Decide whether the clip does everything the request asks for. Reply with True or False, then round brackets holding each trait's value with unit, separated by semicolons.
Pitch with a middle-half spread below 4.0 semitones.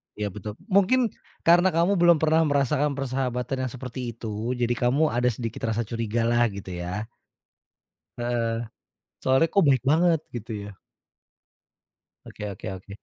False (4.8 semitones)